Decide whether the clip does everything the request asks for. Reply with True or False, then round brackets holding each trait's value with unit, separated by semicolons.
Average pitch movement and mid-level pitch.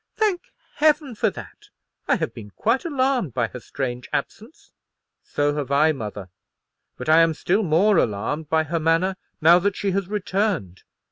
False (7.2 semitones; 165 Hz)